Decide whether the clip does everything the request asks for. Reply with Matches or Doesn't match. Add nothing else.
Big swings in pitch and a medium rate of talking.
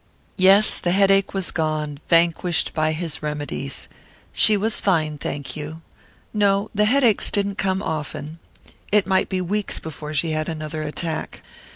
Doesn't match